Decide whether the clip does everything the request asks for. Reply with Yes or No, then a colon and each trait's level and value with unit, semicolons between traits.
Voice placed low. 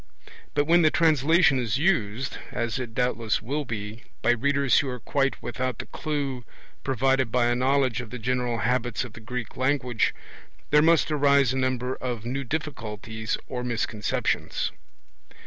Yes: low, 125 Hz